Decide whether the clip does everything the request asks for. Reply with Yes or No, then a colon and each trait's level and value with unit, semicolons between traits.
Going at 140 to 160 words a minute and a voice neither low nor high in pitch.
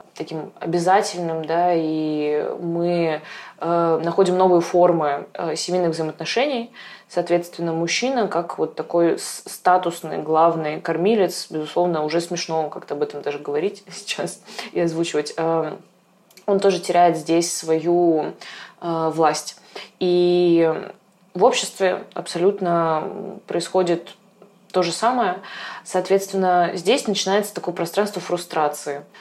No: slow, 110 wpm; medium, 175 Hz